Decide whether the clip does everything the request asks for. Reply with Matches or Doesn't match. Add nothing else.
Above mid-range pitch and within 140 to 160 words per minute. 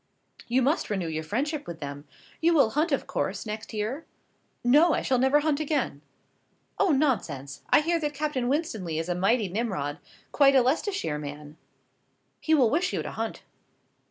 Doesn't match